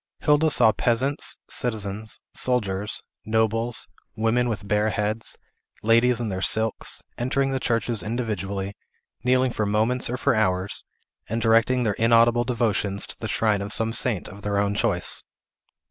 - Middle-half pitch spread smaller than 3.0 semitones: Yes, narrow, 2.6 semitones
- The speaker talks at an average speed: Yes, average, 145 wpm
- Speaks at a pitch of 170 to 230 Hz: No, low, 110 Hz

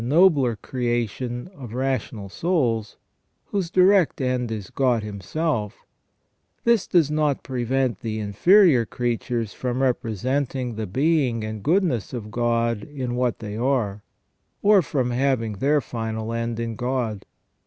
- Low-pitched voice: Yes, low, 125 Hz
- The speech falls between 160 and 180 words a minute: No, slow, 135 wpm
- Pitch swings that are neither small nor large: Yes, average, 3.7 semitones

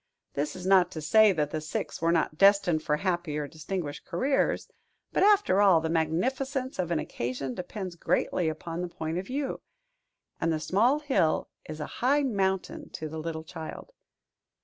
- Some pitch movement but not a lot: Yes, average, 4.3 semitones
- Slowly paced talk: No, average, 175 wpm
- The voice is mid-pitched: Yes, medium, 175 Hz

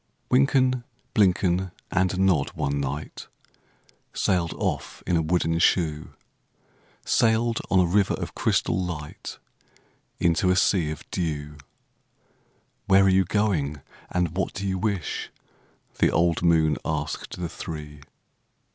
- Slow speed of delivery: Yes, slow, 125 wpm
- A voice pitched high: No, very low, 90 Hz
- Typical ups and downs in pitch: Yes, average, 3.6 semitones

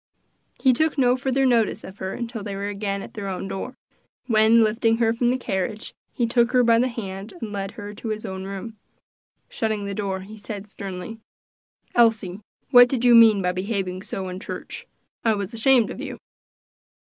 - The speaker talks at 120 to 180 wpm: No, average, 190 wpm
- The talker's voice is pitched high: Yes, high, 215 Hz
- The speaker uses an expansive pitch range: No, average, 3.2 semitones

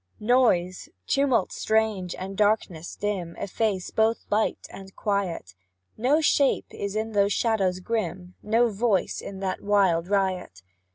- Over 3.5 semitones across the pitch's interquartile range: No, average, 3.1 semitones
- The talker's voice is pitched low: No, high, 200 Hz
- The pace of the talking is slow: Yes, slow, 130 wpm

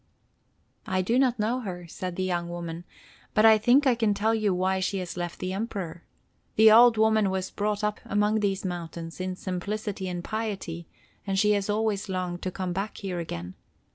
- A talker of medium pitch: No, high, 195 Hz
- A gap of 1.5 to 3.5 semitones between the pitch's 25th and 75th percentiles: Yes, average, 3.2 semitones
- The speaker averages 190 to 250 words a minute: Yes, average, 195 wpm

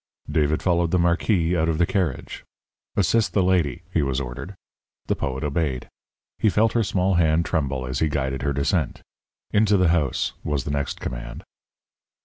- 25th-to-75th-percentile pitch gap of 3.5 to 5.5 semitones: Yes, average, 4.8 semitones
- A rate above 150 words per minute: Yes, average, 170 wpm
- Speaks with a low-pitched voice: Yes, very low, 80 Hz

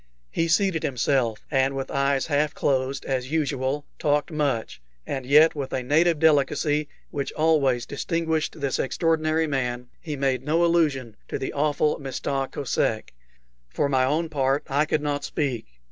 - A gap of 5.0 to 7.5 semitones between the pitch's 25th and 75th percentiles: No, average, 2.7 semitones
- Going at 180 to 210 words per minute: No, average, 155 wpm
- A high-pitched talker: No, medium, 145 Hz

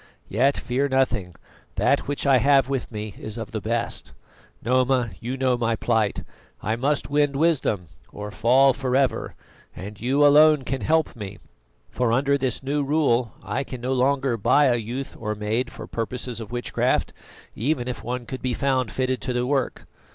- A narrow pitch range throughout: No, average, 3.1 semitones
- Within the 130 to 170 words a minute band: No, average, 180 wpm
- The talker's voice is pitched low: Yes, low, 125 Hz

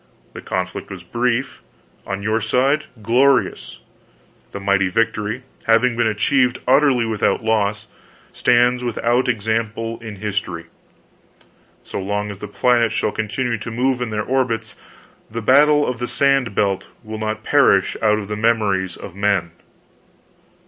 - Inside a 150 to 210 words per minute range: No, average, 140 wpm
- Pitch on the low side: Yes, low, 110 Hz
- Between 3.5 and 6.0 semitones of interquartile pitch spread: No, average, 3.1 semitones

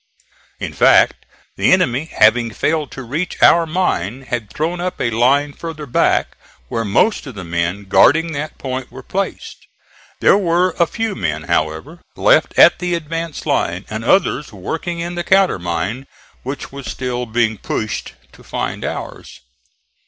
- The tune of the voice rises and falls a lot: Yes, wide, 7.3 semitones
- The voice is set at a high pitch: No, low, 135 Hz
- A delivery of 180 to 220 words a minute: No, average, 155 wpm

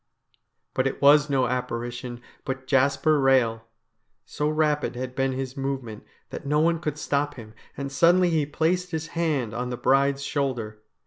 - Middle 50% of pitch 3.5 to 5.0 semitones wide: No, average, 3.0 semitones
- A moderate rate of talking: Yes, average, 165 wpm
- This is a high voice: No, low, 135 Hz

